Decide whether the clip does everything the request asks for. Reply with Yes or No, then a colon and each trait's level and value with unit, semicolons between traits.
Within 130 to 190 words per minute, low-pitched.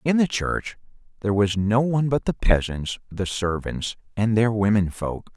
Yes: average, 180 wpm; low, 110 Hz